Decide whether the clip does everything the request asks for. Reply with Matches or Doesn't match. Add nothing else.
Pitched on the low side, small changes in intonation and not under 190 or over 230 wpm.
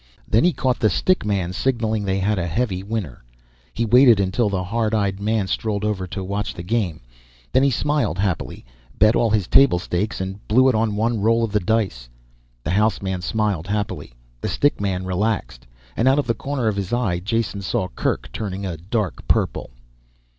Doesn't match